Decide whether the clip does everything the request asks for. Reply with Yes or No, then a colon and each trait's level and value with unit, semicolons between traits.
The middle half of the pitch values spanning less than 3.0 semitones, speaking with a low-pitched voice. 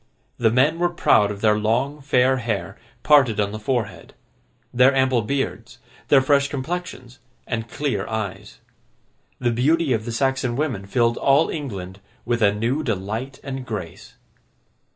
No: average, 4.0 semitones; low, 125 Hz